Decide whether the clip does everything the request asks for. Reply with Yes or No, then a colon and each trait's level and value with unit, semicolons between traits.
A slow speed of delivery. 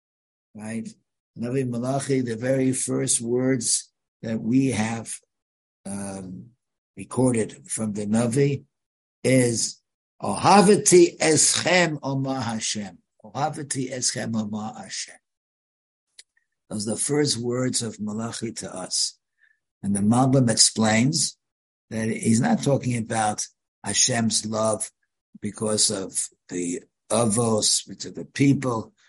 Yes: slow, 105 wpm